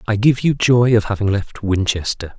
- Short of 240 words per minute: Yes, average, 200 wpm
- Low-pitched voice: Yes, low, 110 Hz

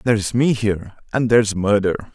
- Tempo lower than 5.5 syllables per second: No, 5.9 syllables/s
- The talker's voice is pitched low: Yes, low, 105 Hz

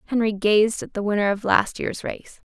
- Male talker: No, female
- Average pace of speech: No, fast, 215 wpm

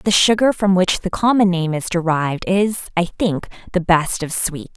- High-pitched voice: No, medium, 180 Hz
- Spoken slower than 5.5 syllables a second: Yes, 4.7 syllables/s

